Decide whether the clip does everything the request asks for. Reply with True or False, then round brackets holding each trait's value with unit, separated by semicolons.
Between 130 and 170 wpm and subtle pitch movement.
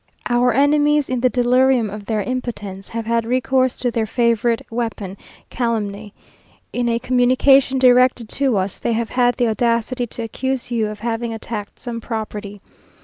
True (160 wpm; 2.3 semitones)